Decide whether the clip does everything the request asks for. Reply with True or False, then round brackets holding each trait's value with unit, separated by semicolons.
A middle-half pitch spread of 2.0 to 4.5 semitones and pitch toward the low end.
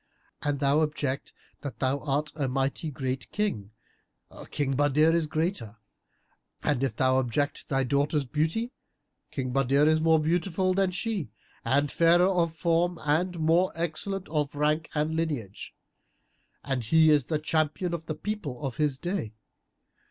False (3.3 semitones; 150 Hz)